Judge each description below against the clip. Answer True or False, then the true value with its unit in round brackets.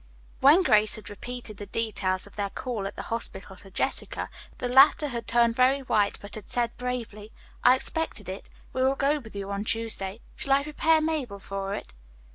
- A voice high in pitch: True (230 Hz)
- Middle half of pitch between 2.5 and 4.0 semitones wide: False (4.5 semitones)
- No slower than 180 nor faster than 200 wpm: True (195 wpm)